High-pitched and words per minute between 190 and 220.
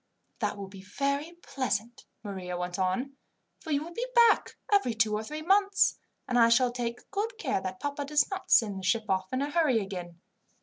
Yes: high, 245 Hz; fast, 205 wpm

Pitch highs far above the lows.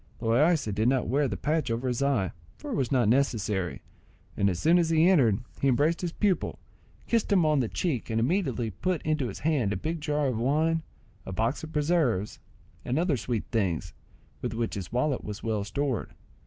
Yes: wide, 5.8 semitones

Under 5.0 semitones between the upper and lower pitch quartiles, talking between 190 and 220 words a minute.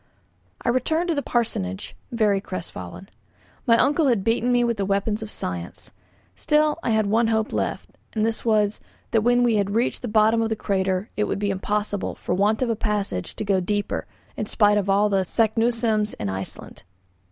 Yes: narrow, 2.6 semitones; average, 195 wpm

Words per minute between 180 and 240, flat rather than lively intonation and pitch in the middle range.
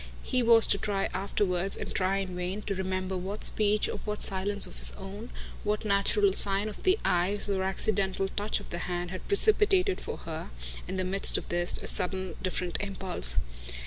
No: average, 190 wpm; narrow, 2.1 semitones; high, 195 Hz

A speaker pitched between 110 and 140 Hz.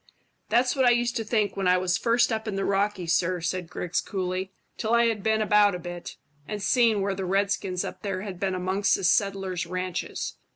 No: high, 195 Hz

